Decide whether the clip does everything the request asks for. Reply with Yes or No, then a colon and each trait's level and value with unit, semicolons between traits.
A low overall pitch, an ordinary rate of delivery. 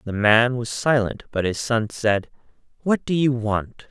Yes: low, 120 Hz; average, 185 wpm